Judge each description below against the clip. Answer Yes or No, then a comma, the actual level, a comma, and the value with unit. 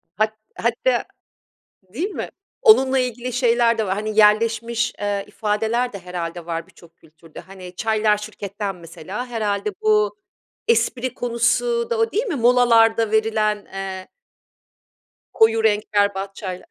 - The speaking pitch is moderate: No, high, 220 Hz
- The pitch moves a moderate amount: Yes, average, 3.5 semitones